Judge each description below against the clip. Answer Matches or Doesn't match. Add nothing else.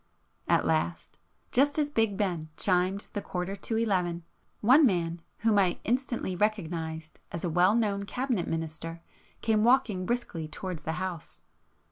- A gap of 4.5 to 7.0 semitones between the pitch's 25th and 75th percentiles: Matches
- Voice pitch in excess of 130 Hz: Matches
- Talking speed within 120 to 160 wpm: Matches